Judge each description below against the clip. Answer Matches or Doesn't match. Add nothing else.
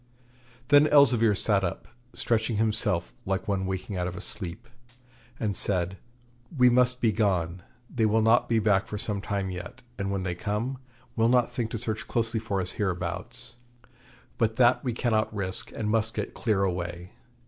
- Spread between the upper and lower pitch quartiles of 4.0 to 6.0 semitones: Doesn't match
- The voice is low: Matches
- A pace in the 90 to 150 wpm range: Doesn't match